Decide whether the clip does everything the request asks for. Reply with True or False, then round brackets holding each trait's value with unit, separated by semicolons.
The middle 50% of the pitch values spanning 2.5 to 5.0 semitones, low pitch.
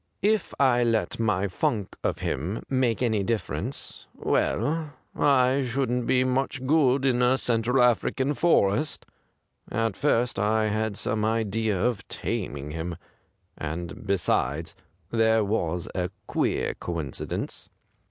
True (4.6 semitones; 115 Hz)